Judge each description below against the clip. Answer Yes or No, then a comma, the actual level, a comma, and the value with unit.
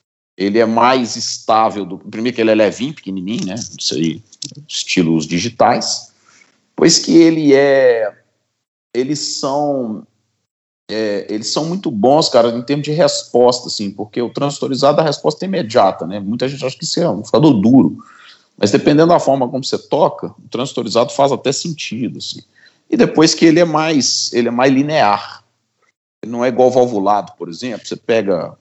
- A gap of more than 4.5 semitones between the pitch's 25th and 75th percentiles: Yes, wide, 5.5 semitones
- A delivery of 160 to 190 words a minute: Yes, average, 170 wpm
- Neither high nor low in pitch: No, low, 125 Hz